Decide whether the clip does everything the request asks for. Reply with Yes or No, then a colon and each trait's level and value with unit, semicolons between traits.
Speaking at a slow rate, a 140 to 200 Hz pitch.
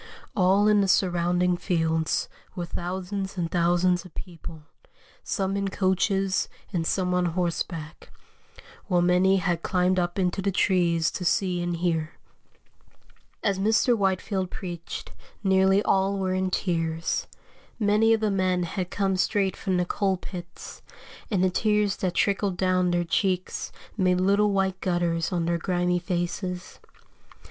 No: average, 145 wpm; medium, 185 Hz